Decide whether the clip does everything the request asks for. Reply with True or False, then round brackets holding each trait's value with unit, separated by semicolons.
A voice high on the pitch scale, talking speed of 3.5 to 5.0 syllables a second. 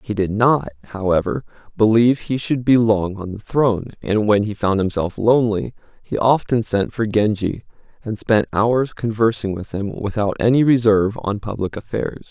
False (110 Hz; 4.9 syllables/s)